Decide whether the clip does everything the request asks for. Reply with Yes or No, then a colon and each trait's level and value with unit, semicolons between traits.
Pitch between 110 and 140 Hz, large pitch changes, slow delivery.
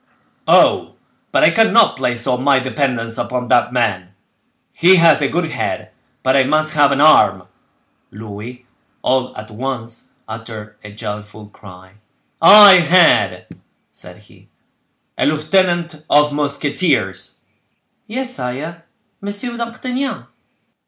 Yes: low, 135 Hz; wide, 7.0 semitones; slow, 120 wpm